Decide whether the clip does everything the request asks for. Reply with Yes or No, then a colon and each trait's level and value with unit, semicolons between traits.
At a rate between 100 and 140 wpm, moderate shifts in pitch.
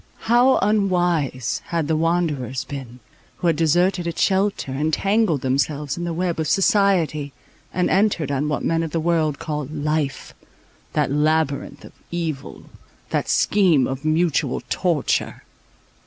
Yes: slow, 135 wpm; average, 3.5 semitones